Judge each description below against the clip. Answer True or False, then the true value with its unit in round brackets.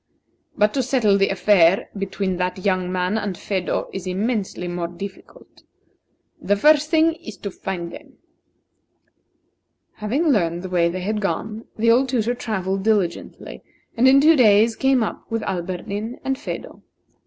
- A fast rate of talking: False (155 wpm)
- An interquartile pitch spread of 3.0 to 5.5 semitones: True (4.1 semitones)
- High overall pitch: True (205 Hz)